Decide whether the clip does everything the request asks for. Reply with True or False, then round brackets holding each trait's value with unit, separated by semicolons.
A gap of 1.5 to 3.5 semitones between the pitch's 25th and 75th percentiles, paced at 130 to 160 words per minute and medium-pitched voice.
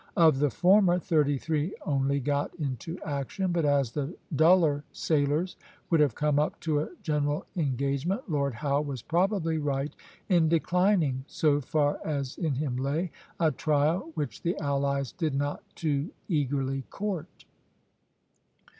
True (2.9 semitones; 145 wpm; 150 Hz)